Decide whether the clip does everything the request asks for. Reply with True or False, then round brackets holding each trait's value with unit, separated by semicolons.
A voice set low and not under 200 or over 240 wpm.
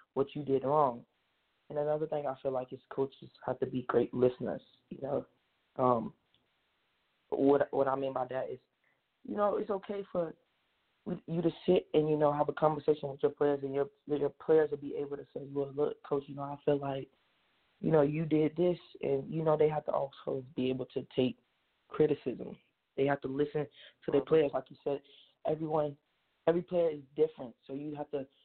False (145 Hz; 205 wpm)